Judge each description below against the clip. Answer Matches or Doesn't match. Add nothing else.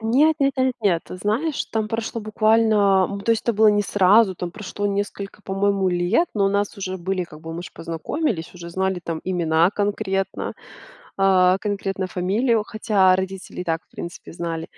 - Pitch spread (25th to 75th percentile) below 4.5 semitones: Matches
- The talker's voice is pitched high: Matches